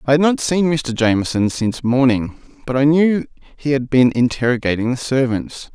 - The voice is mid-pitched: No, low, 130 Hz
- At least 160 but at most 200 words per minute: Yes, average, 180 wpm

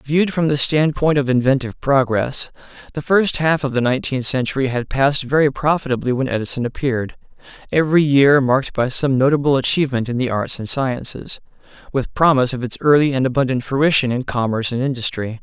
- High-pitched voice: No, low, 135 Hz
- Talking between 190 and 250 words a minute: No, average, 170 wpm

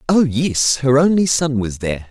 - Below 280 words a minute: Yes, average, 200 wpm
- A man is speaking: Yes, male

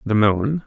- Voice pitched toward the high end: No, low, 115 Hz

